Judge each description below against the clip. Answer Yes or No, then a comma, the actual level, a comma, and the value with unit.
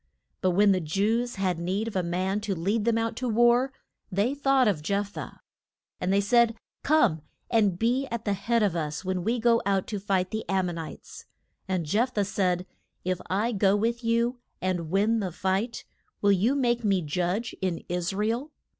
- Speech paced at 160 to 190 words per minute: No, average, 200 wpm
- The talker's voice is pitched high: Yes, high, 200 Hz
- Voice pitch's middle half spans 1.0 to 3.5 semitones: No, average, 3.9 semitones